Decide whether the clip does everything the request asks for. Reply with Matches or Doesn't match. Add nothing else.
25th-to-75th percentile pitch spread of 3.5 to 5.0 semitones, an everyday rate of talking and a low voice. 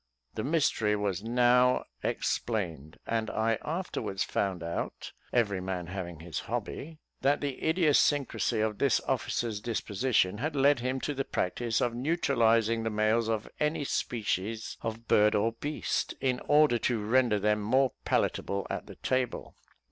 Matches